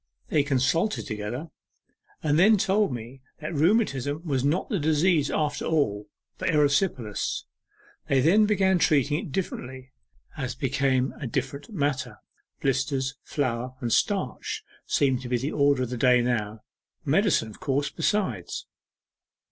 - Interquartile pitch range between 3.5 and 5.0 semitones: Yes, average, 3.9 semitones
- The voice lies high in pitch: No, medium, 140 Hz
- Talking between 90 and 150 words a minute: Yes, average, 140 wpm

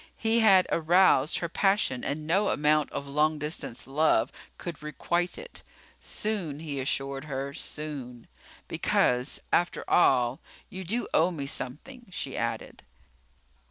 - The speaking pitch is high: No, medium, 155 Hz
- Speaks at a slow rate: Yes, slow, 130 wpm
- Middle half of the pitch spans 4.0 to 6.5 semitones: Yes, average, 4.9 semitones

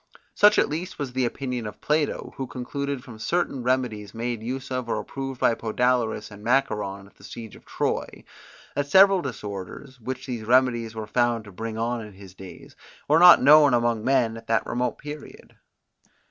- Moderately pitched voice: No, low, 125 Hz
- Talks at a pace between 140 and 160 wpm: No, average, 185 wpm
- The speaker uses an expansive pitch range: No, average, 3.4 semitones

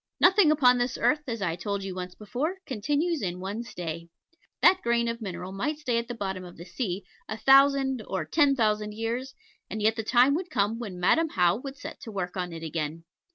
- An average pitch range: No, wide, 6.4 semitones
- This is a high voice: Yes, high, 225 Hz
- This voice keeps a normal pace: No, fast, 215 wpm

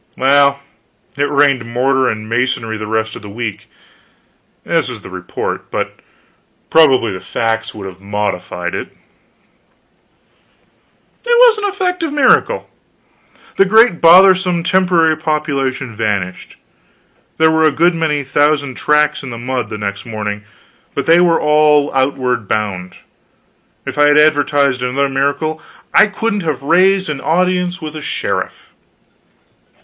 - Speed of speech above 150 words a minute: No, slow, 135 wpm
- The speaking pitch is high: No, medium, 140 Hz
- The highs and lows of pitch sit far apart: Yes, wide, 6.3 semitones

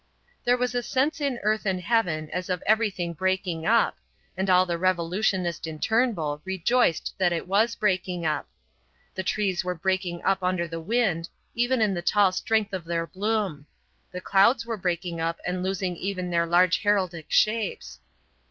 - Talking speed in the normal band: Yes, average, 170 wpm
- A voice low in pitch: No, medium, 185 Hz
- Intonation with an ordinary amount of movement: Yes, average, 3.8 semitones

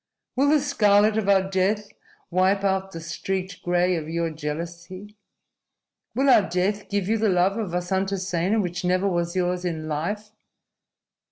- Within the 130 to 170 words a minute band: Yes, average, 155 wpm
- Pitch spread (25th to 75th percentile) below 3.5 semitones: Yes, average, 2.7 semitones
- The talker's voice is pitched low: No, high, 190 Hz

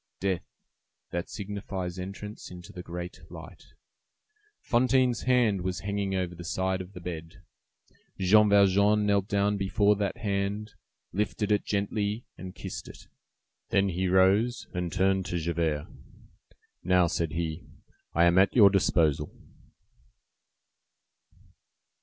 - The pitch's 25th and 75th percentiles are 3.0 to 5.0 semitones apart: No, narrow, 2.5 semitones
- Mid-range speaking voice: No, very low, 95 Hz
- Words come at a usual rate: No, slow, 125 wpm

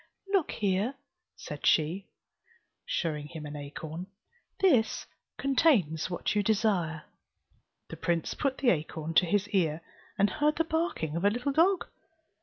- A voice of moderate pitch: No, high, 195 Hz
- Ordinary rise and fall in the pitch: No, wide, 8.6 semitones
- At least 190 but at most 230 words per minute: No, average, 140 wpm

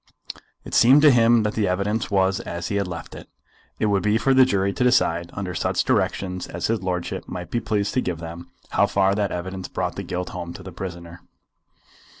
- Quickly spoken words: Yes, fast, 215 wpm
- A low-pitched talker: Yes, very low, 95 Hz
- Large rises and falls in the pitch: No, average, 3.4 semitones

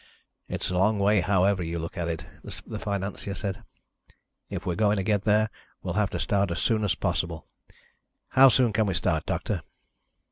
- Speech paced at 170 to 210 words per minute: Yes, average, 185 wpm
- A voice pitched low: Yes, low, 100 Hz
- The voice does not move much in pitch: No, average, 3.1 semitones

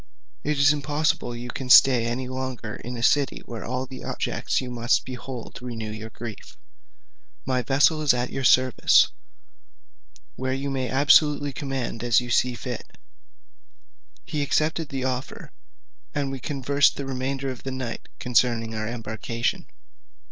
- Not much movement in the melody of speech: Yes, narrow, 2.2 semitones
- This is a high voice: No, low, 130 Hz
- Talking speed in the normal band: Yes, average, 155 wpm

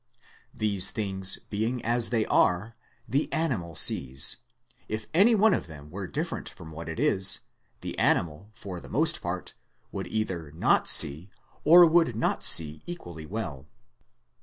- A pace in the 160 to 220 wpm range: No, average, 150 wpm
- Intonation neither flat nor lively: No, wide, 6.2 semitones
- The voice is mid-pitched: No, low, 100 Hz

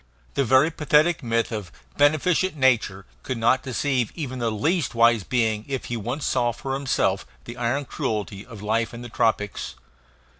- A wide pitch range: No, average, 3.6 semitones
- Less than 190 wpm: Yes, average, 165 wpm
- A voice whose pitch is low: Yes, low, 120 Hz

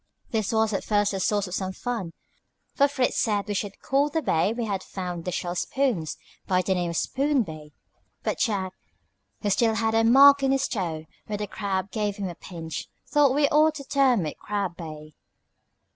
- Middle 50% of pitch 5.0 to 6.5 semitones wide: Yes, wide, 5.6 semitones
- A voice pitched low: No, high, 205 Hz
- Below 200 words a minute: No, fast, 205 wpm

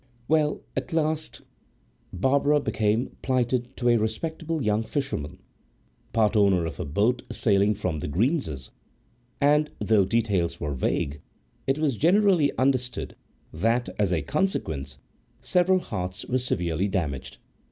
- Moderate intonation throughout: No, wide, 7.7 semitones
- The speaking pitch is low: Yes, low, 115 Hz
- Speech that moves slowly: Yes, slow, 130 wpm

